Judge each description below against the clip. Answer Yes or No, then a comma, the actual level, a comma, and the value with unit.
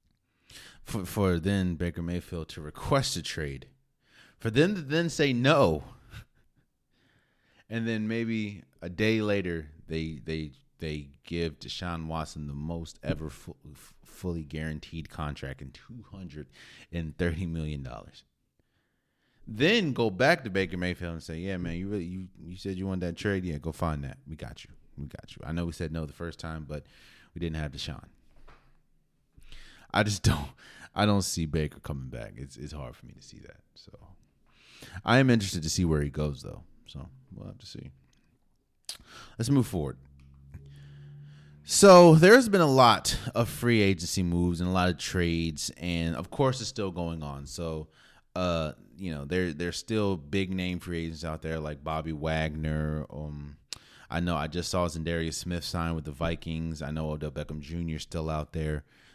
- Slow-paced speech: No, average, 180 wpm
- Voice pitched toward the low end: Yes, very low, 85 Hz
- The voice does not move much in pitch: No, average, 3.6 semitones